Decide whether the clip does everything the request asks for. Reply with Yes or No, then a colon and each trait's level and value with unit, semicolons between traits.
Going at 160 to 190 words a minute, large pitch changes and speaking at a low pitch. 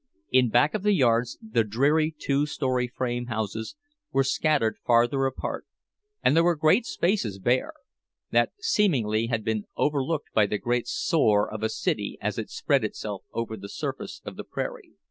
Yes: average, 165 wpm; wide, 5.7 semitones; low, 130 Hz